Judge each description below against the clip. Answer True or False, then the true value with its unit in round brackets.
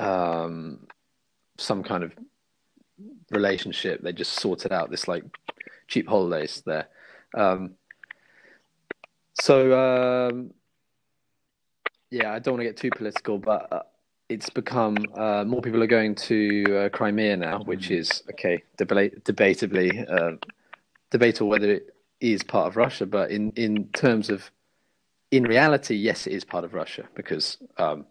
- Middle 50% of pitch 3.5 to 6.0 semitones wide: False (2.8 semitones)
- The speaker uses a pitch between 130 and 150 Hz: False (105 Hz)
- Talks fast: False (145 wpm)